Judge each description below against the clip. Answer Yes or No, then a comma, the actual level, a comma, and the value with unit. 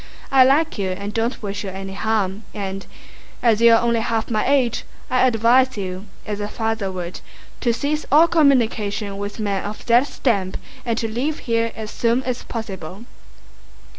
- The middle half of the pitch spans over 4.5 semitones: No, average, 3.3 semitones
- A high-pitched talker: Yes, high, 225 Hz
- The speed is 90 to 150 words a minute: No, average, 165 wpm